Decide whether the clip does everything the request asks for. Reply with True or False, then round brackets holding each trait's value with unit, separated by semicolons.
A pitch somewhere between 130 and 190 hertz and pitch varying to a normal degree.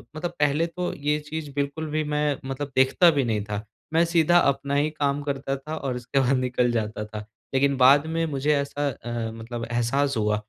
True (140 Hz; 3.4 semitones)